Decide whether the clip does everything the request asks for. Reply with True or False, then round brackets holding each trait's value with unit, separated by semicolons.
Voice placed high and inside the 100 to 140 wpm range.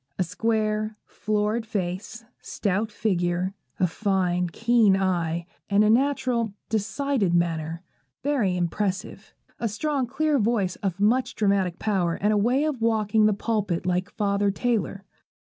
True (205 Hz; 135 wpm)